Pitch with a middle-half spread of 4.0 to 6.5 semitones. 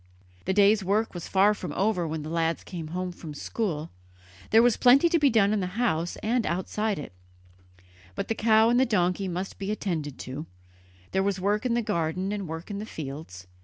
Yes: average, 4.5 semitones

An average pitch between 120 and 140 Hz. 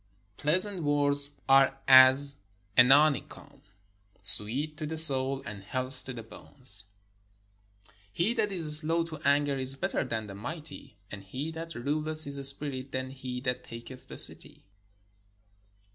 Yes: low, 135 Hz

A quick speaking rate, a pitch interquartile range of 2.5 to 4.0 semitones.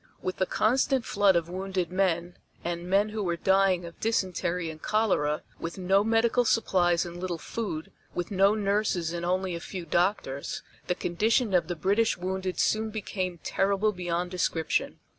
No: average, 165 wpm; average, 2.8 semitones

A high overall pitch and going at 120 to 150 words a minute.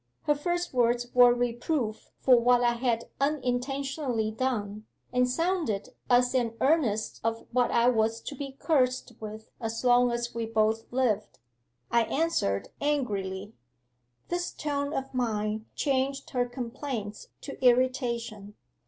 Yes: high, 245 Hz; slow, 135 wpm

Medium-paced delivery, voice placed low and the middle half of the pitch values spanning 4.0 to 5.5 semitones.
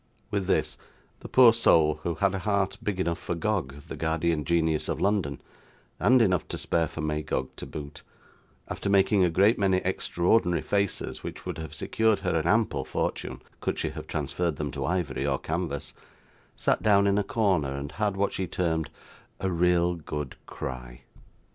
Yes: average, 180 wpm; very low, 85 Hz; average, 4.4 semitones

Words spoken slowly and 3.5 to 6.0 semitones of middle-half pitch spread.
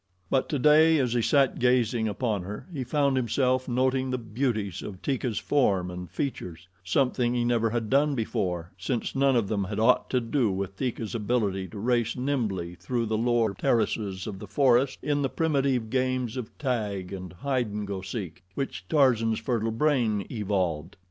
No: average, 175 wpm; average, 4.3 semitones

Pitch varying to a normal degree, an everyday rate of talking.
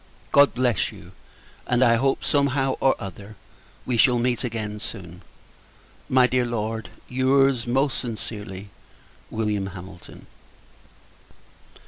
No: average, 3.8 semitones; slow, 110 wpm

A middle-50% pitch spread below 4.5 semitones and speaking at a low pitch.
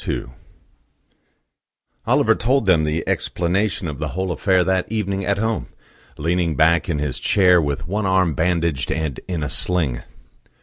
Yes: average, 3.3 semitones; very low, 90 Hz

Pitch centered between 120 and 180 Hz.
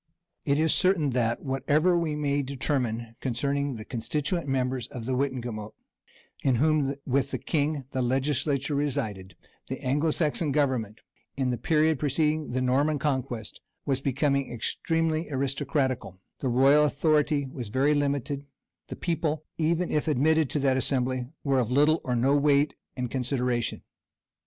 Yes: medium, 140 Hz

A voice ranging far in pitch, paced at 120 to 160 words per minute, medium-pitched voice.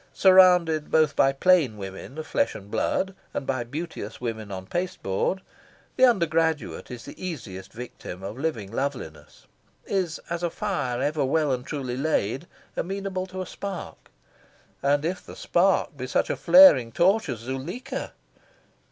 Yes: wide, 6.7 semitones; average, 150 wpm; medium, 150 Hz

